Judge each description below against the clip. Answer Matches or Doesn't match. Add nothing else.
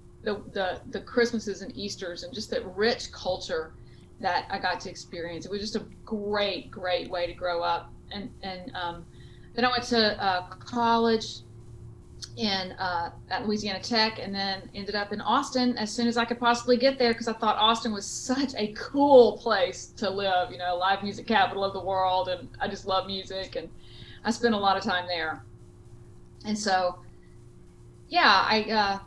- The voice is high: Matches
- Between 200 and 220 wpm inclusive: Doesn't match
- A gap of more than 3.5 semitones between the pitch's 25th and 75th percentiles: Matches